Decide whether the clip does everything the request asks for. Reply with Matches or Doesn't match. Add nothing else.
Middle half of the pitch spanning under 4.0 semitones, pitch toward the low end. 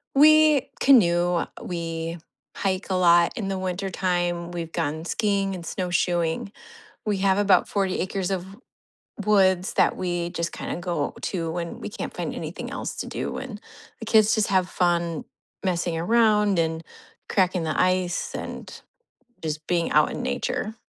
Doesn't match